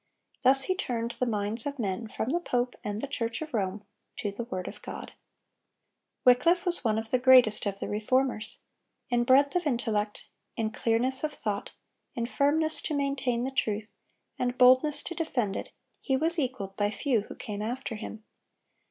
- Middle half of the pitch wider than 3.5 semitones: Yes, average, 4.1 semitones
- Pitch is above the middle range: Yes, high, 245 Hz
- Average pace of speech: Yes, average, 180 wpm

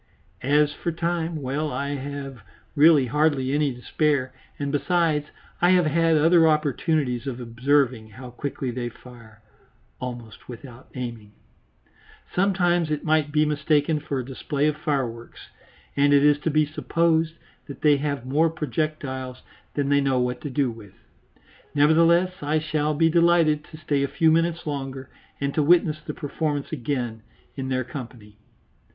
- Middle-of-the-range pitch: Yes, medium, 145 Hz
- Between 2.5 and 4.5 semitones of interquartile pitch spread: Yes, average, 3.3 semitones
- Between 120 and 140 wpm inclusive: No, average, 155 wpm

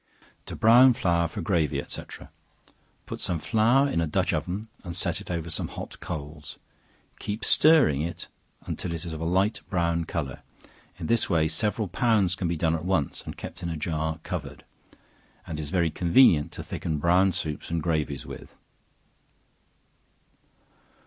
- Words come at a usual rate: Yes, average, 165 wpm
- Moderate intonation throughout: Yes, average, 3.4 semitones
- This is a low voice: Yes, very low, 85 Hz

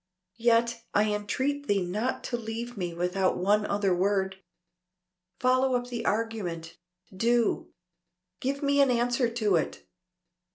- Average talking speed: No, slow, 130 wpm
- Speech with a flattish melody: No, average, 3.9 semitones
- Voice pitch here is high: Yes, high, 225 Hz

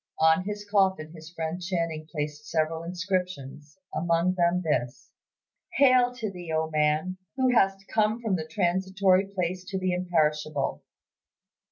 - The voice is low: No, medium, 175 Hz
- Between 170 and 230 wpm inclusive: No, average, 140 wpm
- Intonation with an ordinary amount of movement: Yes, average, 3.3 semitones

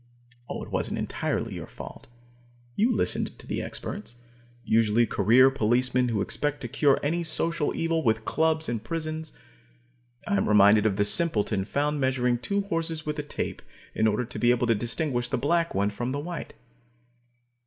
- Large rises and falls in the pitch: Yes, wide, 6.0 semitones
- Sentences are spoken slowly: No, average, 170 wpm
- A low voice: Yes, low, 130 Hz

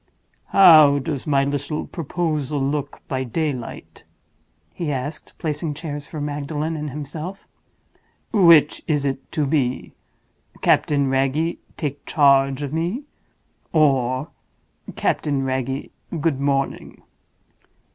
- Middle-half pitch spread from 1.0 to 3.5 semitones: Yes, narrow, 2.4 semitones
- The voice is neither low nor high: Yes, medium, 145 Hz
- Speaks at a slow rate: Yes, slow, 105 wpm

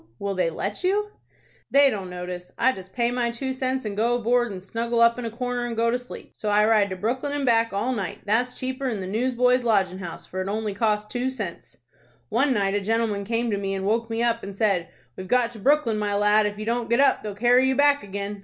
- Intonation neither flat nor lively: Yes, average, 3.5 semitones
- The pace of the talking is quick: Yes, fast, 245 wpm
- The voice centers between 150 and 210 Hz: No, high, 225 Hz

